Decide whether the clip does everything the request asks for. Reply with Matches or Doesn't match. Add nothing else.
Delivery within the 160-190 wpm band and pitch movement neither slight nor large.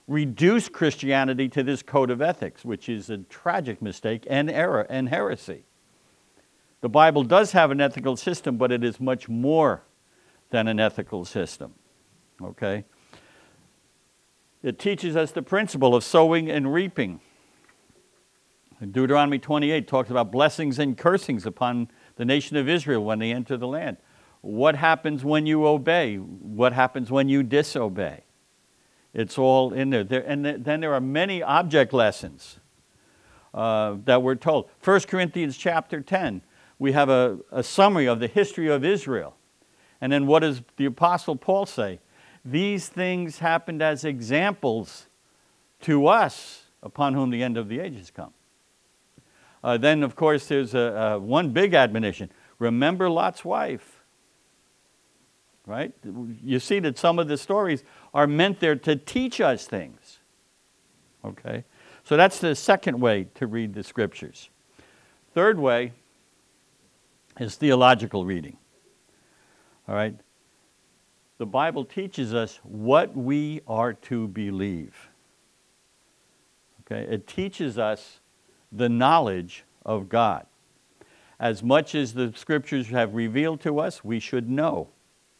Doesn't match